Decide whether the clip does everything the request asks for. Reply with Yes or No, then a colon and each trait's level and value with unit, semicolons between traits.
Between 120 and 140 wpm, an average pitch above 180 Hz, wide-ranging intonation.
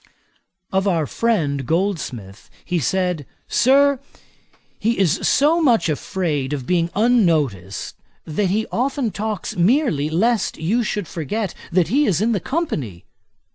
Yes: slow, 135 wpm; high, 190 Hz; wide, 6.8 semitones